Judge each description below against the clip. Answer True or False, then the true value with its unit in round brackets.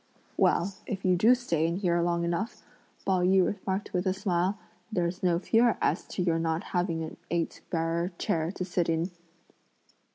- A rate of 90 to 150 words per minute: False (175 wpm)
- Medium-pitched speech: True (180 Hz)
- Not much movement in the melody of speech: True (2.1 semitones)